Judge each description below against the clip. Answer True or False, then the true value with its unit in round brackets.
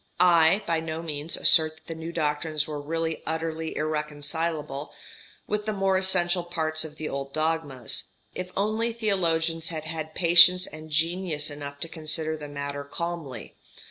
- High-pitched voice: False (160 Hz)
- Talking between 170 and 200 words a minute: False (155 wpm)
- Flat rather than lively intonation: True (2.2 semitones)